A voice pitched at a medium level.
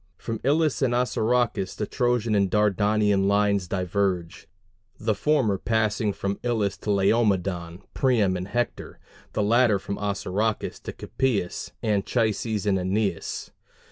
No: low, 105 Hz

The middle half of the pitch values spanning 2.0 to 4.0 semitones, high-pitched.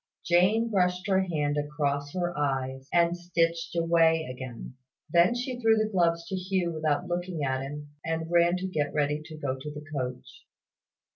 No: average, 3.6 semitones; medium, 165 Hz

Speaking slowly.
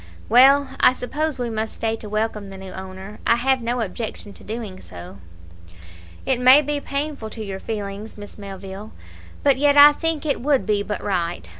No: average, 185 wpm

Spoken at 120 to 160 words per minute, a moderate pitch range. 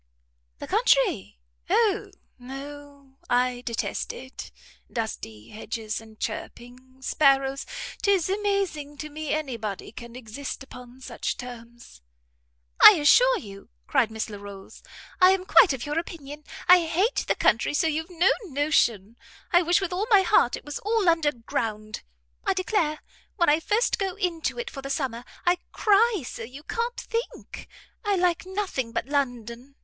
No: average, 150 wpm; wide, 7.0 semitones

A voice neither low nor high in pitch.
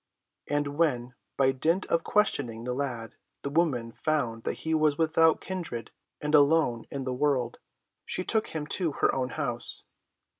Yes: medium, 145 Hz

